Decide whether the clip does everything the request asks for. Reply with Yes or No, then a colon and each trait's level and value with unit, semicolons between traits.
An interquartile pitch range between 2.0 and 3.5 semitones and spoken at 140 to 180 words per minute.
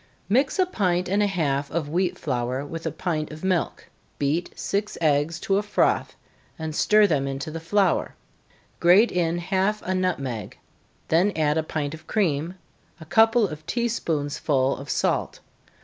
No: average, 4.6 semitones; average, 170 wpm